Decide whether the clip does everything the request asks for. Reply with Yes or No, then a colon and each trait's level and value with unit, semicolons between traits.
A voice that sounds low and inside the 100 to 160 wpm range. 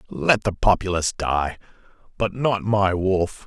Yes: very low, 95 Hz; average, 140 wpm